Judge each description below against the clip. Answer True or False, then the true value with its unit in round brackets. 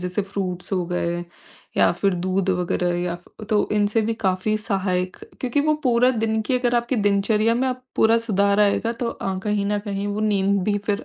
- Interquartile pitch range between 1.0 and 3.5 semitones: True (3.0 semitones)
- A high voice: True (205 Hz)